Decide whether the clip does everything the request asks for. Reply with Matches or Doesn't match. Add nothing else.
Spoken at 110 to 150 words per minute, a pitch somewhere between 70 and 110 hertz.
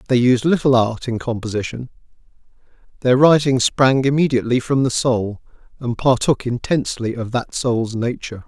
Doesn't match